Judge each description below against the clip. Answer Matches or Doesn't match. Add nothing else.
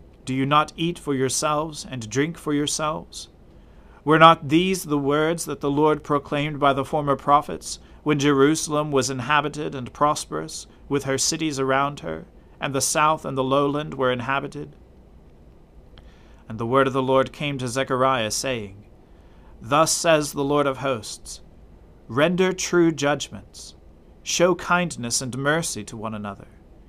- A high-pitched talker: Doesn't match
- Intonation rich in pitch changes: Doesn't match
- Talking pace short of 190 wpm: Matches